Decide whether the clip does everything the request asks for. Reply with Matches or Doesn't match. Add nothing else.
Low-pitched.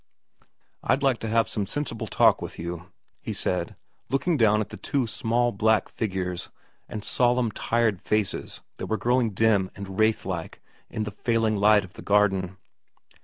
Matches